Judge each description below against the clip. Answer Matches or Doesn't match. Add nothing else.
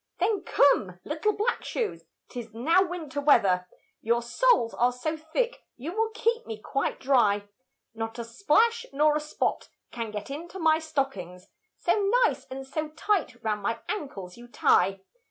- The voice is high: Matches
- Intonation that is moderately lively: Doesn't match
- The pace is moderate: Matches